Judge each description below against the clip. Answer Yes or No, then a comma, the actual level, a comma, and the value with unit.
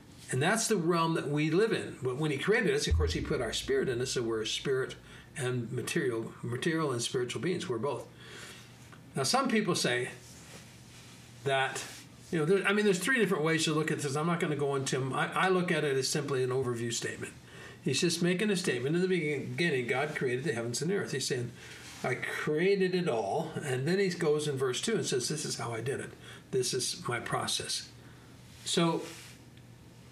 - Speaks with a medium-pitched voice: Yes, medium, 155 Hz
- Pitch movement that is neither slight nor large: No, wide, 6.0 semitones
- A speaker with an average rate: No, fast, 215 wpm